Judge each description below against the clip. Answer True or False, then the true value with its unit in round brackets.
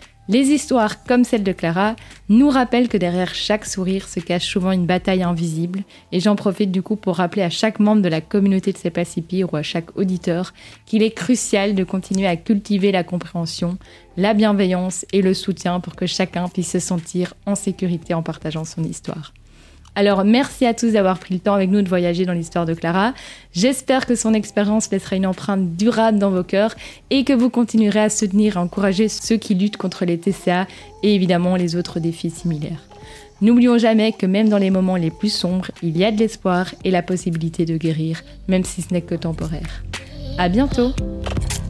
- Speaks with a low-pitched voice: False (190 Hz)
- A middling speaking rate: True (200 wpm)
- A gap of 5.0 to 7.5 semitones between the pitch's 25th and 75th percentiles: False (3.2 semitones)